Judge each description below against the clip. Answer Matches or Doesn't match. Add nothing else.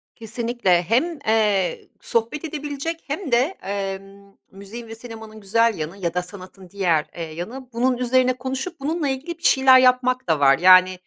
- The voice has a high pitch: Matches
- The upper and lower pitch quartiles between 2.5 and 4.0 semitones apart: Doesn't match